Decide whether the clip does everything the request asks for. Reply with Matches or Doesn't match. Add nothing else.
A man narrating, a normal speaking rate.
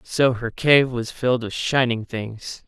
Matches